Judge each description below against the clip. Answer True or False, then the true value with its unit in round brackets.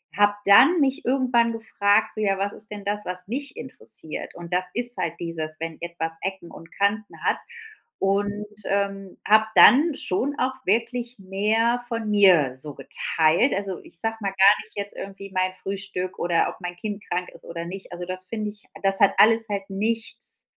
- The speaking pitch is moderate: False (200 Hz)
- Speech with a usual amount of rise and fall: True (3.4 semitones)